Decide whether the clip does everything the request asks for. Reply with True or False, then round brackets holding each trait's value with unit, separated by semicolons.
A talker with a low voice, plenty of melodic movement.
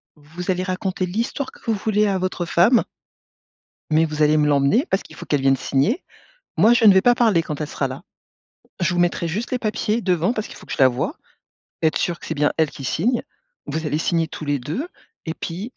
False (175 Hz; 5.8 semitones)